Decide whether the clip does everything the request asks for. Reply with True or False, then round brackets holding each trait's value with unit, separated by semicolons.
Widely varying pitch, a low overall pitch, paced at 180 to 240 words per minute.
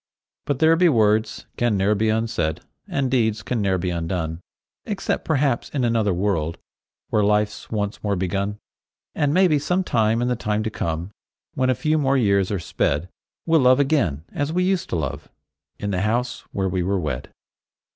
True (5.8 semitones; 110 Hz; 185 wpm)